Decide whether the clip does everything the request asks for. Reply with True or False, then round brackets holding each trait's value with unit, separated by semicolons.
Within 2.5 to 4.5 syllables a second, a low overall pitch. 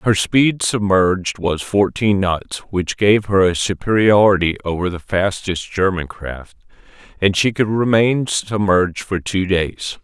True (4.0 syllables/s; 100 Hz)